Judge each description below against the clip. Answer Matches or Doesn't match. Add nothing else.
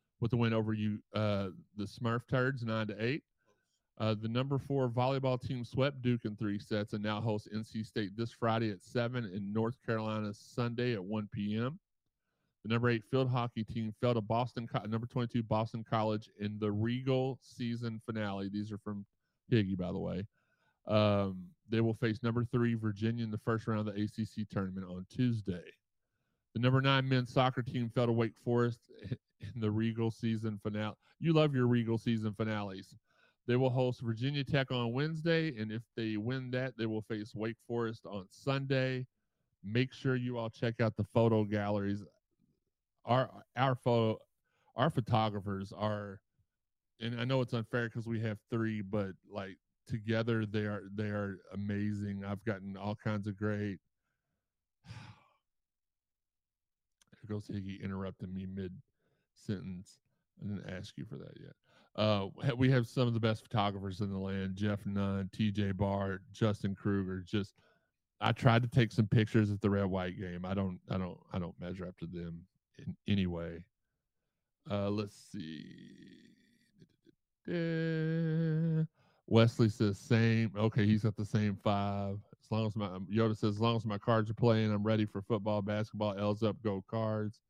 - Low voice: Matches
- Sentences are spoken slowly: Doesn't match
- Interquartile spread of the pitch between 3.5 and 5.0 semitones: Doesn't match